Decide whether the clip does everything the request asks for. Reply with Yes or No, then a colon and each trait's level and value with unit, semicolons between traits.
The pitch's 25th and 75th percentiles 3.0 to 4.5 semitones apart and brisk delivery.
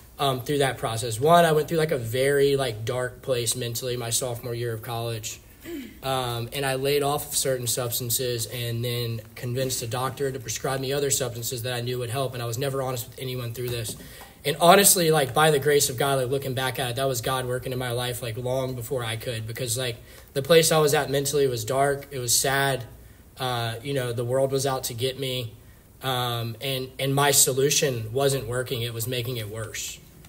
No: narrow, 2.4 semitones; fast, 220 wpm